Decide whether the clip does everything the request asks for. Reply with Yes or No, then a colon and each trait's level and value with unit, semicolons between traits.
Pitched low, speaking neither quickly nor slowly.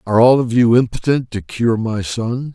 No: low, 115 Hz; fast, 210 wpm